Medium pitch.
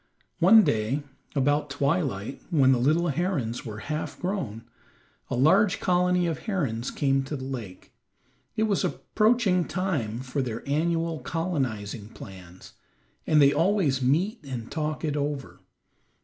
Yes: medium, 145 Hz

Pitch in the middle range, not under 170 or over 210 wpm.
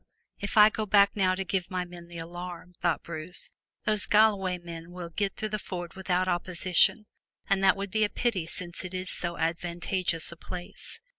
Yes: medium, 180 Hz; average, 195 wpm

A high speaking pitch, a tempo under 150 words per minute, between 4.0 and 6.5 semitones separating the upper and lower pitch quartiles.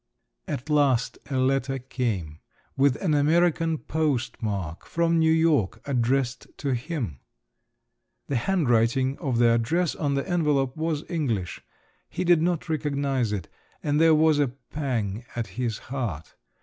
No: low, 135 Hz; slow, 135 wpm; average, 4.8 semitones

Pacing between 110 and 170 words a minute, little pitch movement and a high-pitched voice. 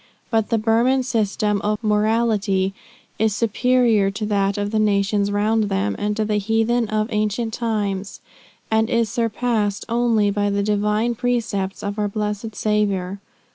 Yes: average, 150 wpm; narrow, 1.8 semitones; high, 210 Hz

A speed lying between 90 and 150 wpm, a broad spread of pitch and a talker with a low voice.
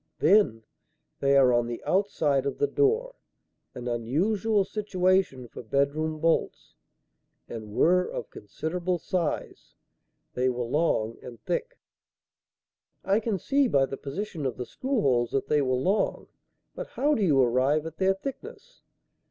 No: average, 145 wpm; wide, 7.3 semitones; medium, 155 Hz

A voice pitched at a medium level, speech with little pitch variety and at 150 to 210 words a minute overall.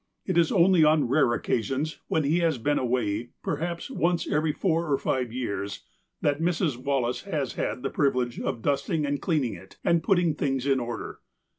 No: medium, 145 Hz; average, 4.6 semitones; average, 180 wpm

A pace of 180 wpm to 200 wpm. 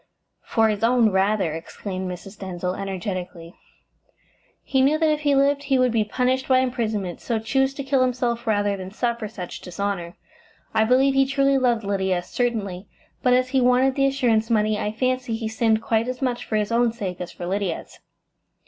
Yes: average, 185 wpm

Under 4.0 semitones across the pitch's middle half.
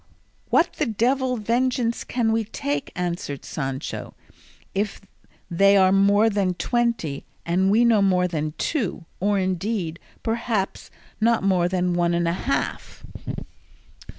No: average, 4.6 semitones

